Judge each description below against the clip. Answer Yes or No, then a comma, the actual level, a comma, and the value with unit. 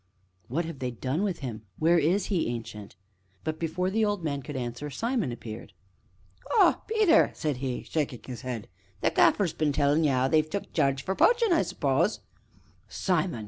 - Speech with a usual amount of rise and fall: No, wide, 6.2 semitones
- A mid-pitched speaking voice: Yes, medium, 155 Hz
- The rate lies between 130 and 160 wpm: No, average, 185 wpm